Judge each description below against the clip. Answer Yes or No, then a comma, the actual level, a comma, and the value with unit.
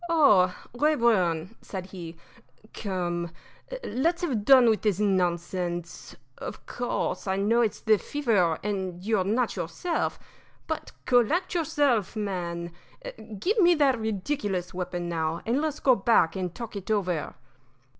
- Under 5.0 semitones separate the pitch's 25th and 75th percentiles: No, wide, 5.5 semitones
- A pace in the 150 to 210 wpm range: No, slow, 135 wpm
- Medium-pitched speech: No, high, 205 Hz